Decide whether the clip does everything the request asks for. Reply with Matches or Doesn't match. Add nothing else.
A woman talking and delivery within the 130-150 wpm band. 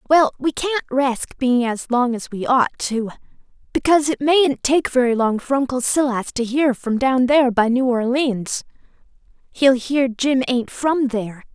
Doesn't match